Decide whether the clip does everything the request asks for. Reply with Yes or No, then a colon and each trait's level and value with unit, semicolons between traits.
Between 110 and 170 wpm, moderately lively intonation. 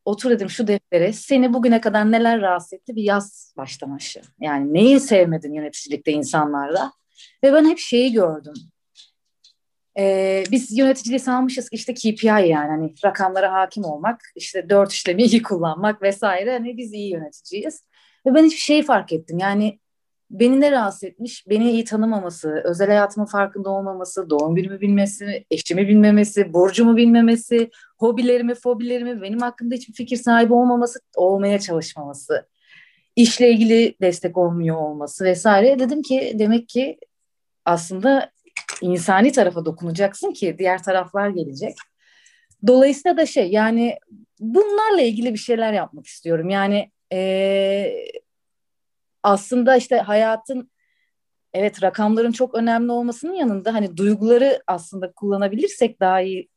Yes: average, 130 wpm; average, 4.4 semitones